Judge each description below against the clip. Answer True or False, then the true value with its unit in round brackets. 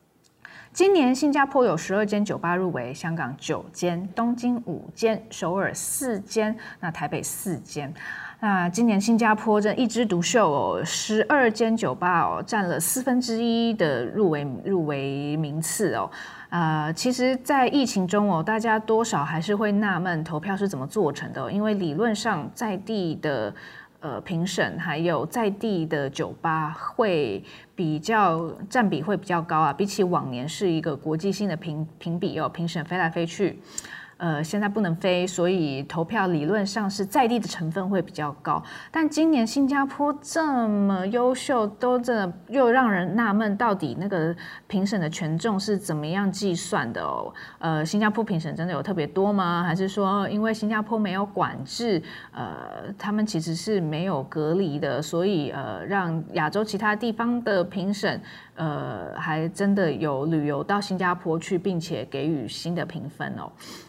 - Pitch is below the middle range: False (195 Hz)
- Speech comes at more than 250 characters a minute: False (245 characters per minute)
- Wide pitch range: False (4.8 semitones)